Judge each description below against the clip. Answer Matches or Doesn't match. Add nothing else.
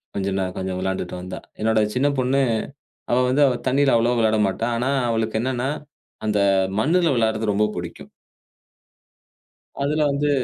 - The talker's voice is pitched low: Matches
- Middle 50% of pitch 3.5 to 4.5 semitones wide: Matches